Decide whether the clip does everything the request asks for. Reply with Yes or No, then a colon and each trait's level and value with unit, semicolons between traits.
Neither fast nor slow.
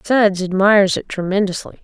No: slow, 130 wpm